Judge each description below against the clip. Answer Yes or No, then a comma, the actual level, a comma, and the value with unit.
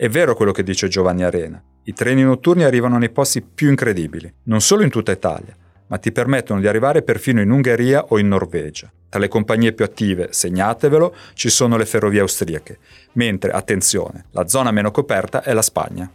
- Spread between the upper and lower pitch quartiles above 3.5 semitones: Yes, average, 5.2 semitones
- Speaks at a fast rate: Yes, fast, 190 wpm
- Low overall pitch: Yes, low, 110 Hz